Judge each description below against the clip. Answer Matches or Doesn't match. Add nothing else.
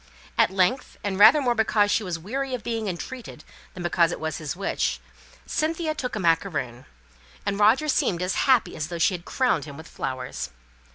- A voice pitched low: Doesn't match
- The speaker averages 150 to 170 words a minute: Doesn't match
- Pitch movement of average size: Doesn't match